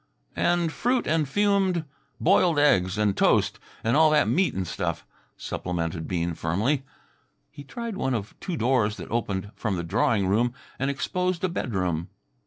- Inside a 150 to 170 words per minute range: Yes, average, 160 wpm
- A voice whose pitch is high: No, low, 125 Hz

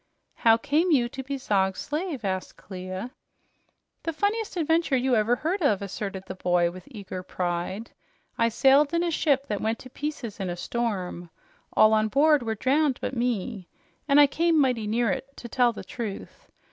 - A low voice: No, high, 240 Hz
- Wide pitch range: Yes, wide, 6.3 semitones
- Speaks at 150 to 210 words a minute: Yes, average, 185 wpm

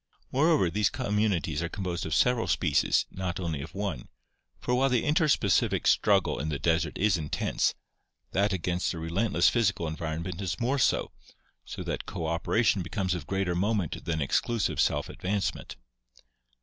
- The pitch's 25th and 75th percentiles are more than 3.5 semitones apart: Yes, average, 4.4 semitones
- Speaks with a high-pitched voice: No, very low, 95 Hz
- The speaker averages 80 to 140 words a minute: No, average, 155 wpm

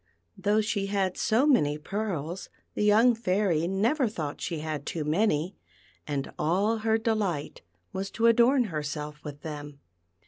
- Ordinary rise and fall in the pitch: No, wide, 6.4 semitones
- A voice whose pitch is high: Yes, high, 195 Hz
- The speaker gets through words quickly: No, average, 145 wpm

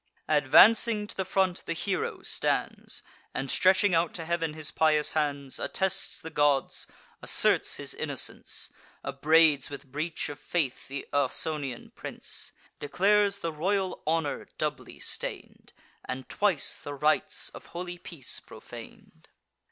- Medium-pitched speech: Yes, medium, 160 Hz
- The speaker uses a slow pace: Yes, slow, 130 wpm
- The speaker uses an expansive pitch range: No, average, 4.2 semitones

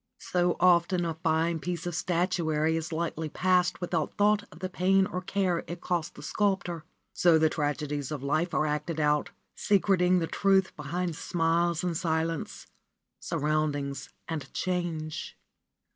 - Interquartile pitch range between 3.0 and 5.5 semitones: No, narrow, 2.4 semitones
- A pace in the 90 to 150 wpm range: Yes, average, 145 wpm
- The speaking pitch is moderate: Yes, medium, 170 Hz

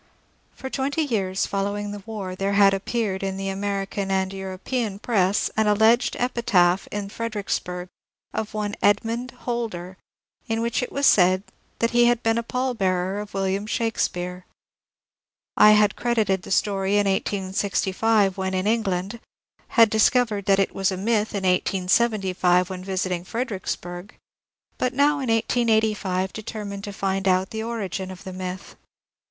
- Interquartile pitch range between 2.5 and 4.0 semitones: Yes, average, 3.0 semitones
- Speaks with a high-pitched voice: Yes, high, 200 Hz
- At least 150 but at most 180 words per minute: Yes, average, 155 wpm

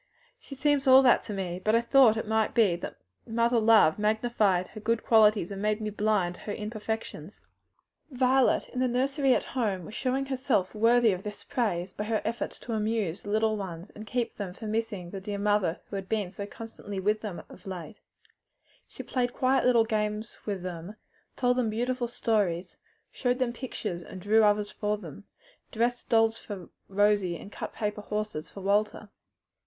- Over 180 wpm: Yes, average, 190 wpm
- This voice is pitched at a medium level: No, high, 215 Hz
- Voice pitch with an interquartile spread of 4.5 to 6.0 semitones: No, average, 2.8 semitones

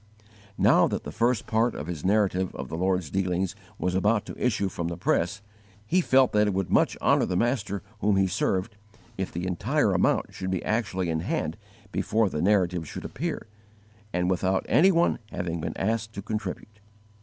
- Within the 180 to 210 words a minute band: Yes, average, 190 wpm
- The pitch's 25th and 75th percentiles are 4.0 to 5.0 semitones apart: No, average, 3.2 semitones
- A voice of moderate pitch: No, very low, 95 Hz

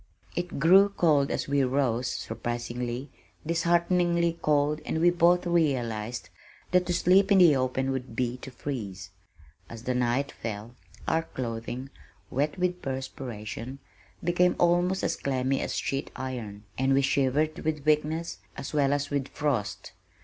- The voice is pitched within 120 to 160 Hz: Yes, medium, 140 Hz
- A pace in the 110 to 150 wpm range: Yes, average, 145 wpm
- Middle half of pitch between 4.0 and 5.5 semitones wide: Yes, average, 5.2 semitones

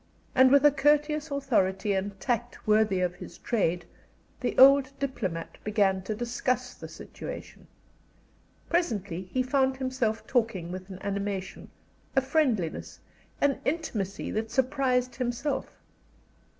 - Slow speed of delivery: Yes, slow, 125 wpm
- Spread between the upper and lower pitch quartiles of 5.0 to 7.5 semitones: Yes, average, 5.3 semitones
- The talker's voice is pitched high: Yes, high, 240 Hz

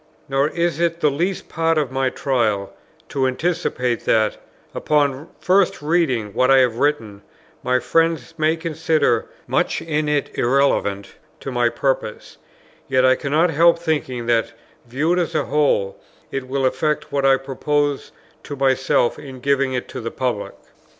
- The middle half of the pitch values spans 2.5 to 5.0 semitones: Yes, average, 3.5 semitones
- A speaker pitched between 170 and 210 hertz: No, low, 135 Hz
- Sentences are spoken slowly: No, average, 155 wpm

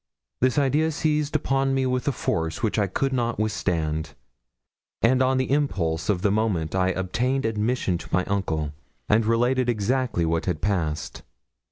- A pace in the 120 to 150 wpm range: No, average, 165 wpm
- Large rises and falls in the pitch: Yes, wide, 6.2 semitones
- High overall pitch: No, low, 110 Hz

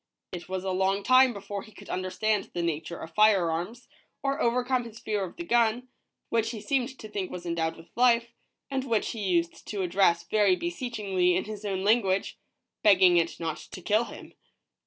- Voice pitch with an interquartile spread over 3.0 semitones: Yes, average, 4.4 semitones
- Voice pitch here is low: No, high, 205 Hz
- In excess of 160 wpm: Yes, average, 195 wpm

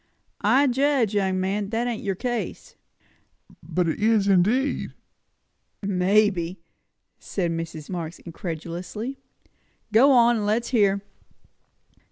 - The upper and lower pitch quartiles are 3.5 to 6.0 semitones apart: Yes, average, 4.6 semitones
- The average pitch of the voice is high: Yes, high, 200 Hz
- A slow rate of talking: Yes, slow, 110 wpm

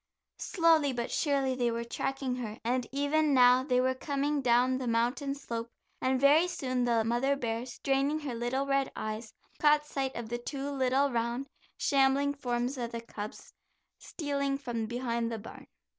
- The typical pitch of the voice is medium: No, very high, 260 Hz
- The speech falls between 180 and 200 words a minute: No, average, 170 wpm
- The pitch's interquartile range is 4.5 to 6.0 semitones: No, average, 2.8 semitones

